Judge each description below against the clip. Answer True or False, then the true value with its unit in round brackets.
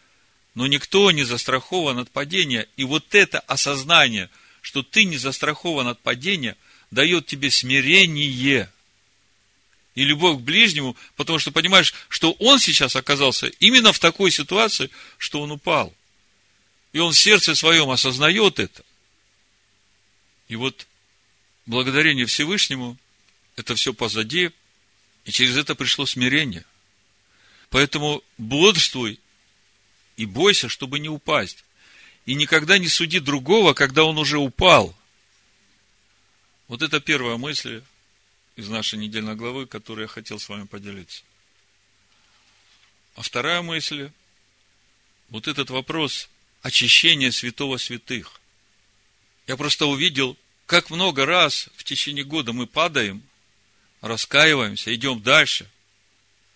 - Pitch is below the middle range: True (125 Hz)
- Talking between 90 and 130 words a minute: True (115 wpm)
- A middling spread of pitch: False (6.3 semitones)